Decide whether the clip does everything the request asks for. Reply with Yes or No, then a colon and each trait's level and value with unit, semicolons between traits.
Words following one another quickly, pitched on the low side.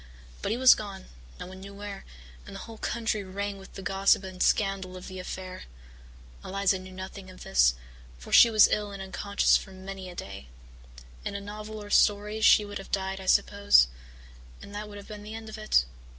No: fast, 210 wpm; high, 200 Hz